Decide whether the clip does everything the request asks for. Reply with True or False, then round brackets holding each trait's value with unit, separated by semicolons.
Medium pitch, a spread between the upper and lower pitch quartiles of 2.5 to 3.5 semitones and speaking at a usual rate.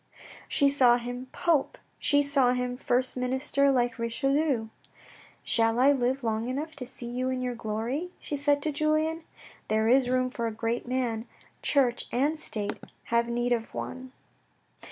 False (255 Hz; 2.8 semitones; 175 wpm)